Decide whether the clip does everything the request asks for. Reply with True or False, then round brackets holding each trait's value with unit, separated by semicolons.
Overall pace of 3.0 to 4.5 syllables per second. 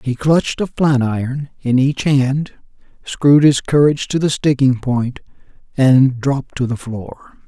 True (4.3 syllables/s)